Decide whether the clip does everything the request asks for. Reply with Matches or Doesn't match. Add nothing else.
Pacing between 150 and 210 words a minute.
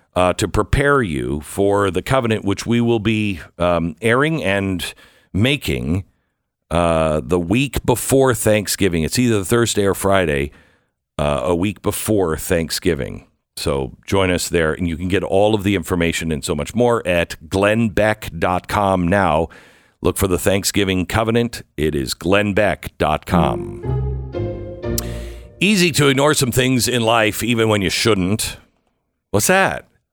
Doesn't match